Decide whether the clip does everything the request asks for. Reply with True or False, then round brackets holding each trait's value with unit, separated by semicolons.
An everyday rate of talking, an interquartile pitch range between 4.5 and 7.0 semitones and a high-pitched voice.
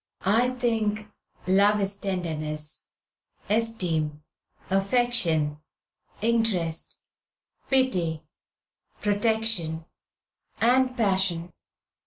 False (60 wpm; 5.5 semitones; 200 Hz)